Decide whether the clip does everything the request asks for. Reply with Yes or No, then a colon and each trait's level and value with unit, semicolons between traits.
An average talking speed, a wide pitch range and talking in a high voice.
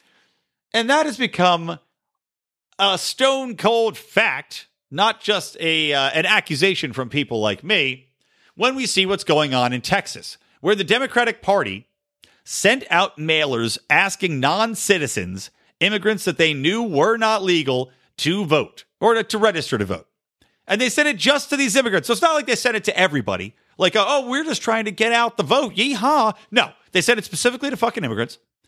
Yes: average, 180 wpm; wide, 7.3 semitones; high, 200 Hz